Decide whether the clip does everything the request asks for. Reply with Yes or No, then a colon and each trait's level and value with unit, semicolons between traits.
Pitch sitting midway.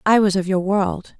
No: high, 195 Hz